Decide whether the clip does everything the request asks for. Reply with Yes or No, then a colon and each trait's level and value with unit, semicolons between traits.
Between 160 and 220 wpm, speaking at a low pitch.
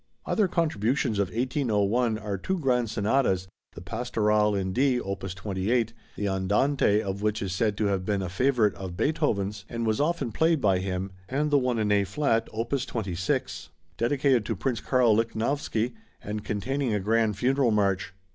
Yes: average, 170 wpm; low, 110 Hz